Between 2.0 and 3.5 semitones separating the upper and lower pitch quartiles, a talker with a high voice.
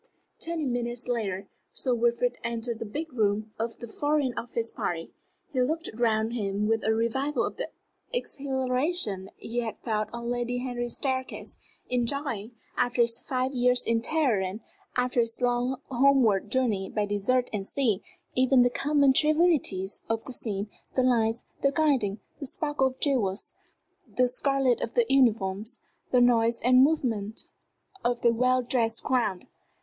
Yes: average, 2.8 semitones; high, 245 Hz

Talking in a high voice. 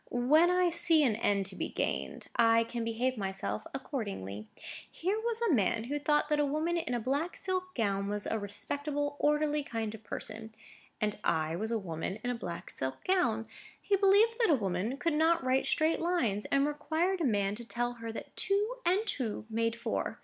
Yes: very high, 250 Hz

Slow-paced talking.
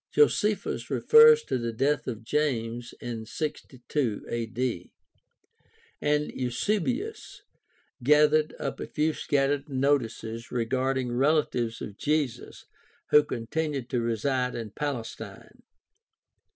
Yes: slow, 105 wpm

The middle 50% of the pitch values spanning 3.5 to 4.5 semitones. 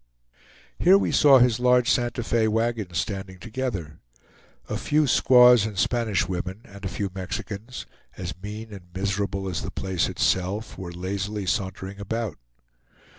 Yes: average, 3.8 semitones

